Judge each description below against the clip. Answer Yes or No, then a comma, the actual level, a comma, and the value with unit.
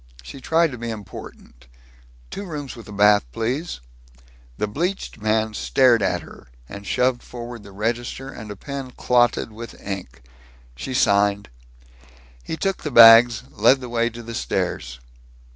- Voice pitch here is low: Yes, low, 115 Hz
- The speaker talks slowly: No, average, 150 wpm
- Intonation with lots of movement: No, average, 3.8 semitones